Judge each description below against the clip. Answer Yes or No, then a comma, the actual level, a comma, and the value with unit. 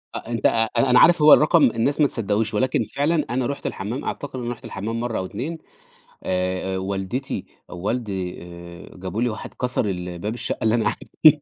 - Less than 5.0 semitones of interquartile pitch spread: No, average, 5.3 semitones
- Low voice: Yes, low, 115 Hz